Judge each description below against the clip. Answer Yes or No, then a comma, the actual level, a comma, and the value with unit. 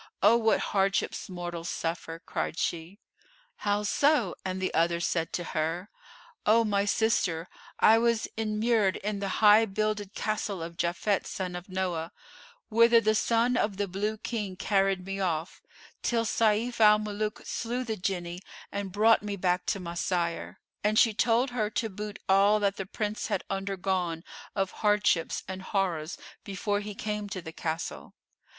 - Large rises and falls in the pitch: No, average, 3.0 semitones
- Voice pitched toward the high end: Yes, high, 200 Hz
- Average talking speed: Yes, average, 160 wpm